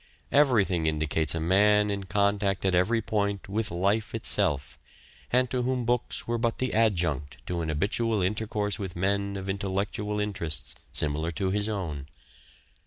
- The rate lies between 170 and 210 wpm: No, average, 155 wpm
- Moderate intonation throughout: Yes, average, 3.7 semitones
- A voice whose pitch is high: No, low, 100 Hz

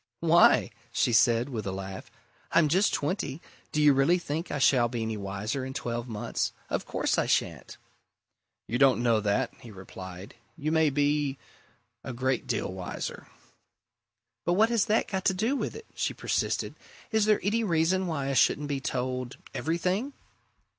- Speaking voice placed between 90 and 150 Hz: Yes, medium, 140 Hz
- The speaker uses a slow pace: No, average, 170 wpm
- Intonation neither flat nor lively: No, wide, 6.5 semitones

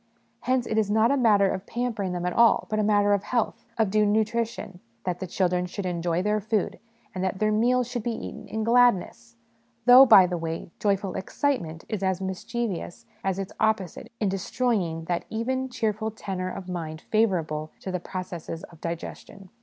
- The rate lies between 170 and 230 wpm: Yes, average, 190 wpm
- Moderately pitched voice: No, high, 200 Hz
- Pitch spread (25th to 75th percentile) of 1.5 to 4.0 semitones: Yes, average, 3.7 semitones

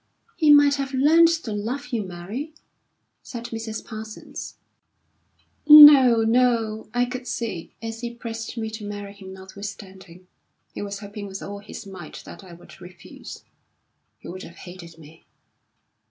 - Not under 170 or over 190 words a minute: No, average, 150 wpm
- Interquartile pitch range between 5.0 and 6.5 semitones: No, average, 4.2 semitones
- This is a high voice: Yes, high, 220 Hz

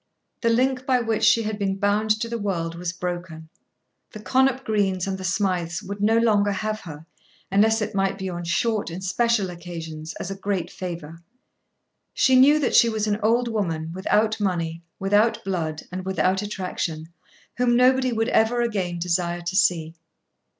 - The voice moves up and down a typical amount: Yes, average, 4.2 semitones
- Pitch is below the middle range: No, high, 195 Hz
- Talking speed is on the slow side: No, average, 175 wpm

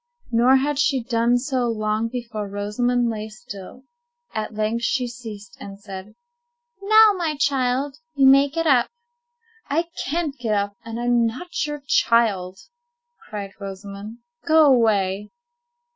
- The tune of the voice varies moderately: Yes, average, 4.3 semitones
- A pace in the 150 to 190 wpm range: No, slow, 135 wpm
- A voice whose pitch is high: Yes, high, 235 Hz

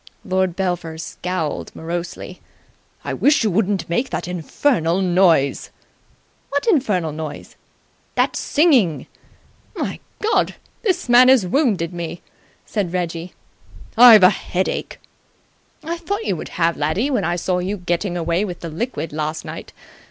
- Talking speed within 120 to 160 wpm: Yes, slow, 135 wpm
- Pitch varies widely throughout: Yes, wide, 5.8 semitones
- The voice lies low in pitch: No, medium, 180 Hz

